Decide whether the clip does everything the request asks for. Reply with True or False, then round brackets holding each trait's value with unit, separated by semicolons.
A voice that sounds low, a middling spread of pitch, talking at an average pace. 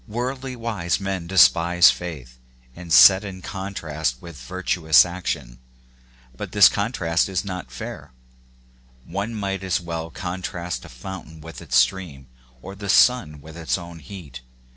True (90 Hz; 3.3 semitones; 145 wpm)